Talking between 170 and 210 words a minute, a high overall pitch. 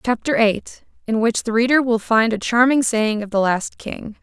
Yes: average, 200 wpm; high, 225 Hz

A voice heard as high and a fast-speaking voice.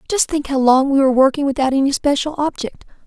Yes: very high, 275 Hz; fast, 215 wpm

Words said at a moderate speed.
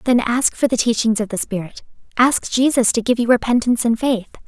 No: fast, 215 wpm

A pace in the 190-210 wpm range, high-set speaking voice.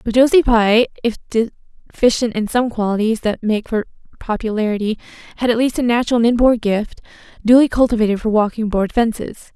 No: average, 165 wpm; high, 225 Hz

